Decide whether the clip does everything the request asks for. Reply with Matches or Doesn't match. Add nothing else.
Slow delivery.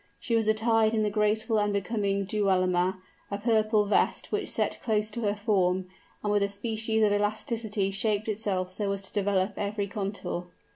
Doesn't match